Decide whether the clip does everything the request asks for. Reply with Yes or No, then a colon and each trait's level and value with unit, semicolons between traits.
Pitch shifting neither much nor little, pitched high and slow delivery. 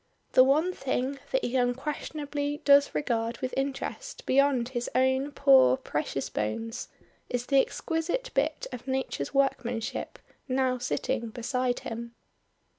Yes: average, 3.0 semitones; very high, 260 Hz; slow, 125 wpm